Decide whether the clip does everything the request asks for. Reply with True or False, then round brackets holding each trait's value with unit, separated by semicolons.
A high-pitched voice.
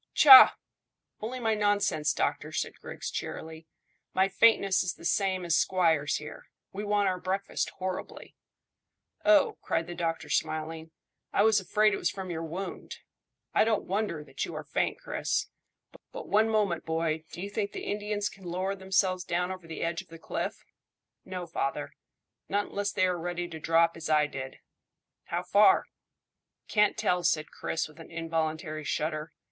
False (180 Hz)